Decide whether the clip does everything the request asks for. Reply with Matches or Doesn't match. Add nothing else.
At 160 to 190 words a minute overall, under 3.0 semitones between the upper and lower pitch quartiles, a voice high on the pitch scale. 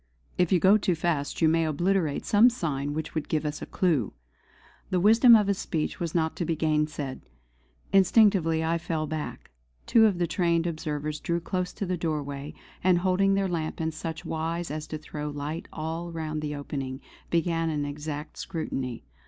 Doesn't match